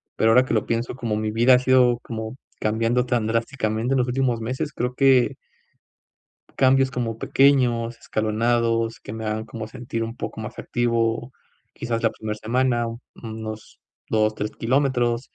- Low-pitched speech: Yes, low, 115 Hz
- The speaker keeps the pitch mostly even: Yes, narrow, 2.0 semitones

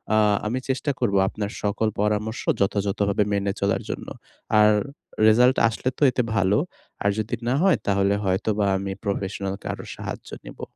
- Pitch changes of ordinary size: No, narrow, 1.9 semitones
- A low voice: Yes, low, 105 Hz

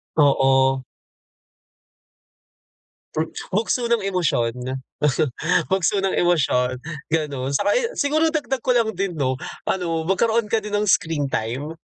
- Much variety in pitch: Yes, wide, 8.3 semitones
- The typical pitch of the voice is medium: Yes, medium, 170 Hz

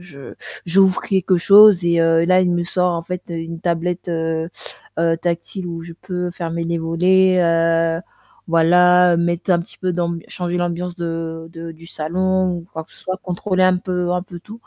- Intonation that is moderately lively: No, narrow, 1.6 semitones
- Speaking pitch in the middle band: Yes, medium, 175 Hz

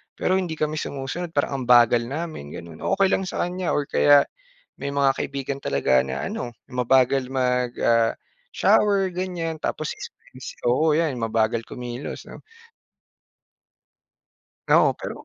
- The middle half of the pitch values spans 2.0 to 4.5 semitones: No, average, 5.2 semitones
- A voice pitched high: No, medium, 140 Hz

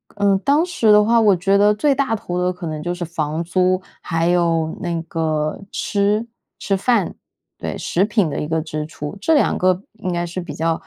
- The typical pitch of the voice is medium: Yes, medium, 180 Hz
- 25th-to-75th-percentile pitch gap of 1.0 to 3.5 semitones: No, average, 4.0 semitones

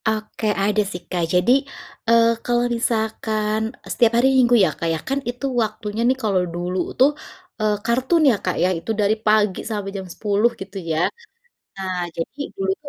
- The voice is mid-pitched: No, high, 215 Hz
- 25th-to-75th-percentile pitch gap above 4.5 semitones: No, average, 3.4 semitones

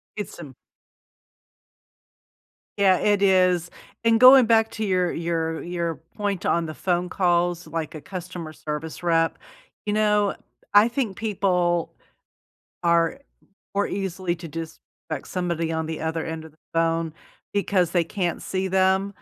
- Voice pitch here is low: No, medium, 180 Hz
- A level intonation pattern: No, average, 3.2 semitones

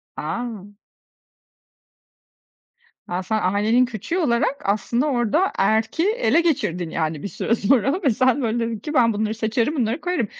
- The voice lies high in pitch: Yes, high, 230 Hz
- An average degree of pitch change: Yes, average, 4.5 semitones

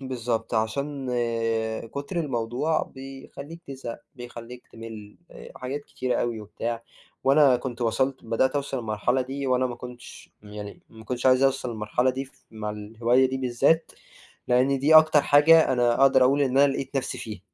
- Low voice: Yes, low, 130 Hz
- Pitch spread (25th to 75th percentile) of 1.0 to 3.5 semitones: Yes, average, 2.8 semitones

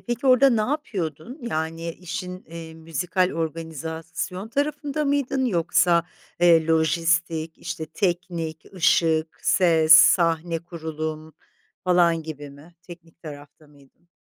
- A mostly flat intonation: Yes, narrow, 2.2 semitones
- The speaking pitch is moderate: Yes, medium, 165 Hz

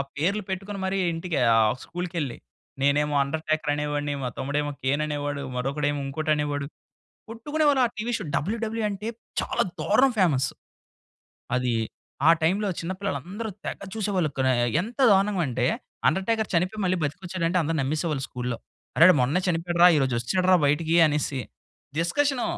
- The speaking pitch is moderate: Yes, medium, 165 Hz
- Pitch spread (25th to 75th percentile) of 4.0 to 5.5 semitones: Yes, average, 5.2 semitones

